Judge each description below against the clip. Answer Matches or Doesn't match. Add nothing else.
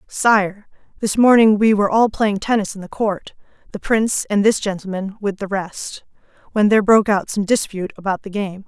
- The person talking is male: Doesn't match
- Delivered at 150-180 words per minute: Doesn't match